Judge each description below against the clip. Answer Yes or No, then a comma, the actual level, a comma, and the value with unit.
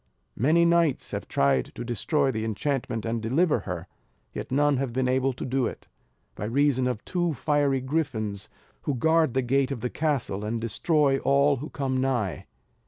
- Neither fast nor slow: Yes, average, 175 wpm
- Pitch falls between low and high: No, low, 130 Hz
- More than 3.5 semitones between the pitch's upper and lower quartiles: Yes, average, 4.0 semitones